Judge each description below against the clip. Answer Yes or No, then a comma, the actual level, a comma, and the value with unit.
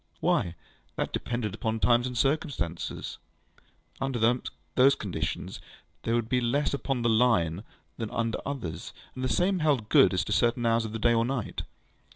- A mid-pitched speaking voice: No, low, 120 Hz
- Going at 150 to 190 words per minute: Yes, average, 170 wpm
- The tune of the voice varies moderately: Yes, average, 3.0 semitones